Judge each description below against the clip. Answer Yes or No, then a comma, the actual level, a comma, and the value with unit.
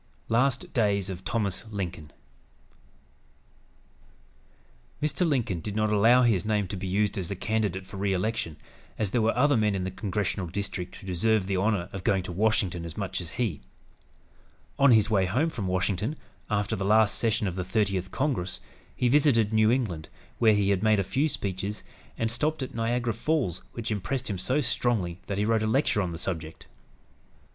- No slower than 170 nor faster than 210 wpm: Yes, average, 185 wpm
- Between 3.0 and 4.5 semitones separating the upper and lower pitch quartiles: Yes, average, 3.5 semitones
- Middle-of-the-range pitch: No, low, 105 Hz